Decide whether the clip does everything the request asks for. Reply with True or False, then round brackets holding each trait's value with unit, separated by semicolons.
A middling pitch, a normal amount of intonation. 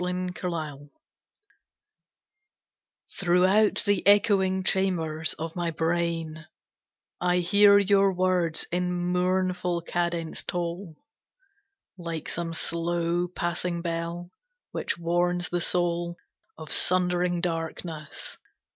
False (175 Hz; 1.3 semitones)